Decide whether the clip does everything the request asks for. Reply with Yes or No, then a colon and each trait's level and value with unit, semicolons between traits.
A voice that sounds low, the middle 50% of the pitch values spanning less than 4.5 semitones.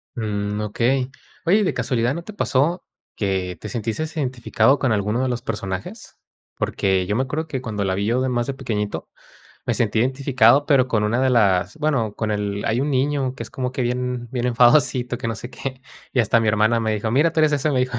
Yes: low, 120 Hz; average, 3.8 semitones